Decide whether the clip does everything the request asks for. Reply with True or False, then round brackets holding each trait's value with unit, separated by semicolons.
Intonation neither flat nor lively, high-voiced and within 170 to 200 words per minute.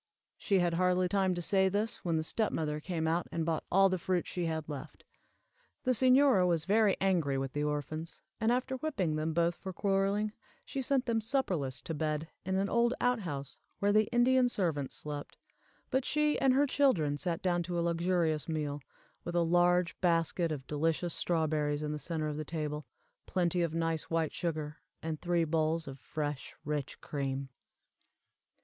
False (4.1 semitones; 170 Hz; 180 wpm)